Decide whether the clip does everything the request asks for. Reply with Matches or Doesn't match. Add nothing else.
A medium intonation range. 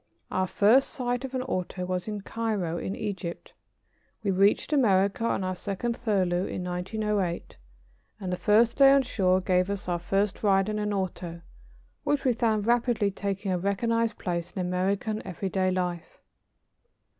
Matches